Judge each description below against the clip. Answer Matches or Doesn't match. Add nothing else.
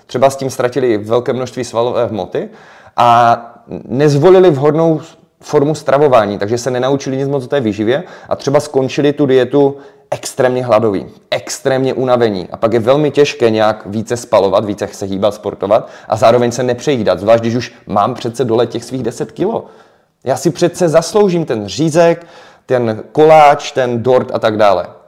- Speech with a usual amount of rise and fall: Matches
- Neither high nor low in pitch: Doesn't match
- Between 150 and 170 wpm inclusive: Matches